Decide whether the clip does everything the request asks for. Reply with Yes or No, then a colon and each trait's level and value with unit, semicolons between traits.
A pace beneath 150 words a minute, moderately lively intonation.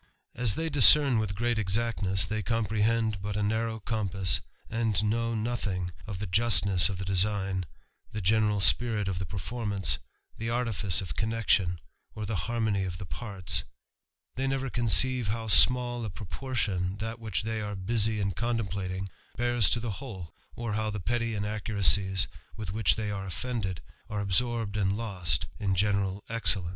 No: average, 160 wpm; average, 3.1 semitones